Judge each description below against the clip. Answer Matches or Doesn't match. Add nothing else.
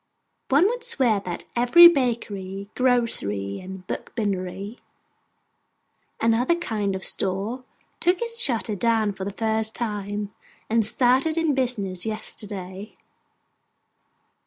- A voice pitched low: Doesn't match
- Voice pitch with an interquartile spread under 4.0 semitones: Doesn't match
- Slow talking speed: Matches